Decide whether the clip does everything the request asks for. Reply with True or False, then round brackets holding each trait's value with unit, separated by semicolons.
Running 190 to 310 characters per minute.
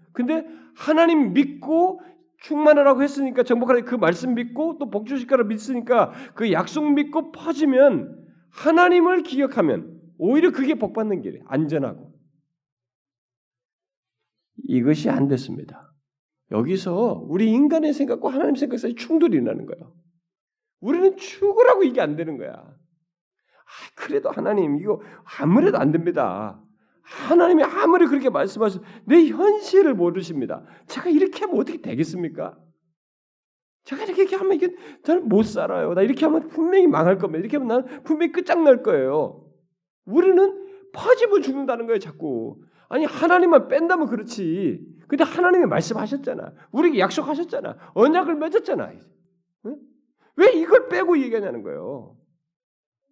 False (330 characters per minute)